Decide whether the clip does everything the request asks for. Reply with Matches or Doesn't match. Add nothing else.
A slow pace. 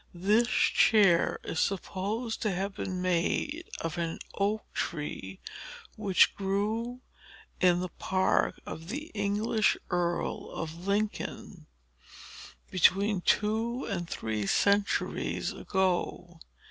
Matches